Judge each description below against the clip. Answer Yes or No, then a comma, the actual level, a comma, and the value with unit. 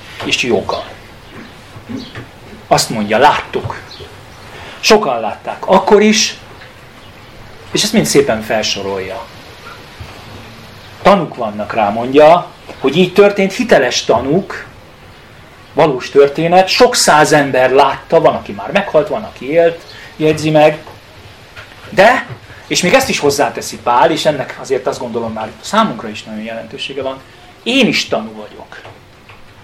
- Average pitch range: No, wide, 7.1 semitones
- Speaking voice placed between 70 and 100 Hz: No, low, 130 Hz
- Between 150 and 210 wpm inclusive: No, average, 120 wpm